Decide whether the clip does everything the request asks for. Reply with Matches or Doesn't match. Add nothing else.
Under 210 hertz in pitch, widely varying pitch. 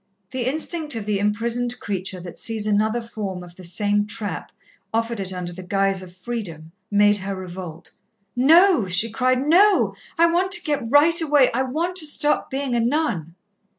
Doesn't match